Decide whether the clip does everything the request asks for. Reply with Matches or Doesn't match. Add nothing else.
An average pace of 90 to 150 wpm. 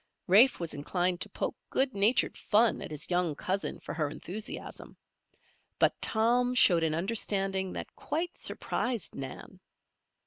Matches